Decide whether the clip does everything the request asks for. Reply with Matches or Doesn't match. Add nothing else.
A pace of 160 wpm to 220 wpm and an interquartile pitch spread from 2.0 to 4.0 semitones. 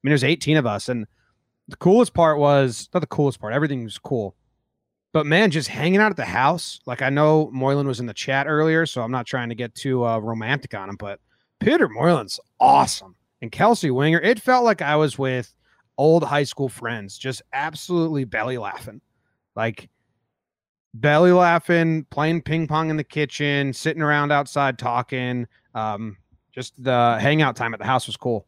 Doesn't match